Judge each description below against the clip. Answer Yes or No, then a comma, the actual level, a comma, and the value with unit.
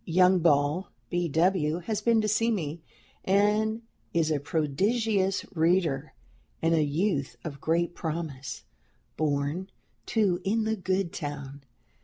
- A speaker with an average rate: No, slow, 130 wpm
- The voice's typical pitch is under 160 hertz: No, medium, 170 Hz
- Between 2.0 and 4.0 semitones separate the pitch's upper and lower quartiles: No, average, 4.7 semitones